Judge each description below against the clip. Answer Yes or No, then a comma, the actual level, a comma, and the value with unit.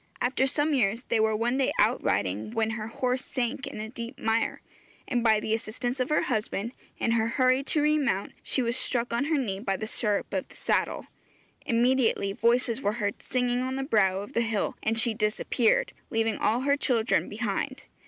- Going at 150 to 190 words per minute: No, average, 200 wpm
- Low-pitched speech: No, high, 235 Hz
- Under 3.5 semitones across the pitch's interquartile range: Yes, average, 3.0 semitones